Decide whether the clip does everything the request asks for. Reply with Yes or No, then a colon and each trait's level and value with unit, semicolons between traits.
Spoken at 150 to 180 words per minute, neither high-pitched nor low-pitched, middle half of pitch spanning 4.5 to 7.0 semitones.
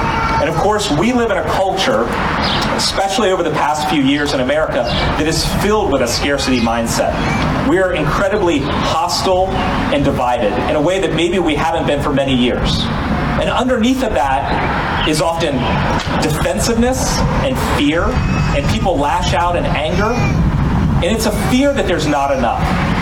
Yes: average, 165 wpm; medium, 165 Hz; wide, 5.4 semitones